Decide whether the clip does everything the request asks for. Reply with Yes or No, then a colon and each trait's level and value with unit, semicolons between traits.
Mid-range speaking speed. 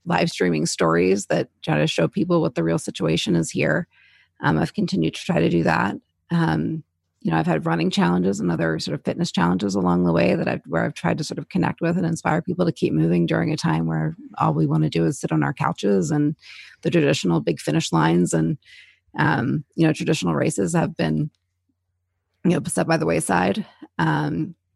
No: fast, 215 wpm